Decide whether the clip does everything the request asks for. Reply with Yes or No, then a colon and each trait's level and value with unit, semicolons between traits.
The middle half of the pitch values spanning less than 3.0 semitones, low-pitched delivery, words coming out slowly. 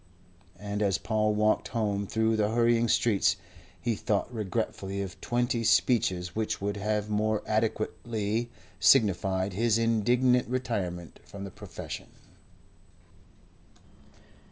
Yes: narrow, 2.5 semitones; low, 110 Hz; slow, 110 wpm